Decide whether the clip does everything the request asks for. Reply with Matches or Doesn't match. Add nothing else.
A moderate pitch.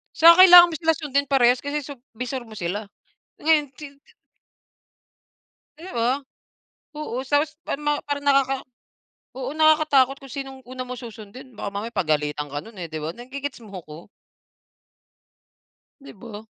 Doesn't match